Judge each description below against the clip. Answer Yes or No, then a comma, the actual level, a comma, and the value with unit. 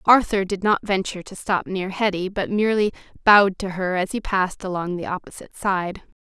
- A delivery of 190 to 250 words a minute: Yes, average, 195 wpm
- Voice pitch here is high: Yes, high, 195 Hz